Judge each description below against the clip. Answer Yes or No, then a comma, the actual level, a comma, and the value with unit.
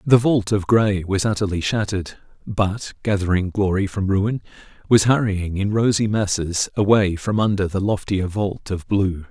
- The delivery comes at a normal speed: Yes, average, 160 wpm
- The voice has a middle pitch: No, low, 100 Hz